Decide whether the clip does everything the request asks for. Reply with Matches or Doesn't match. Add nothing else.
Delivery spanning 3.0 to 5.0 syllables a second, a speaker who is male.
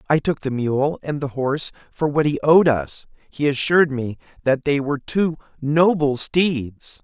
Matches